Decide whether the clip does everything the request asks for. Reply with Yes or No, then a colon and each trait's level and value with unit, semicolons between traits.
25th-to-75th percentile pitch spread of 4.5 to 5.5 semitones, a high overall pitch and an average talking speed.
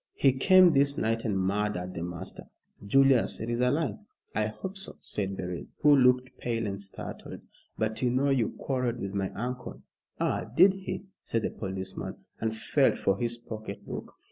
No: average, 4.9 semitones; low, 115 Hz; average, 180 wpm